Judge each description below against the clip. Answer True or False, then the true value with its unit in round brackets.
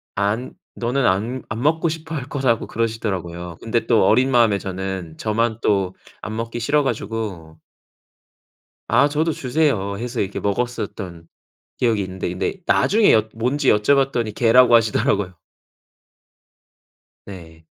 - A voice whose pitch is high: False (115 Hz)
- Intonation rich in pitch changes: False (4.7 semitones)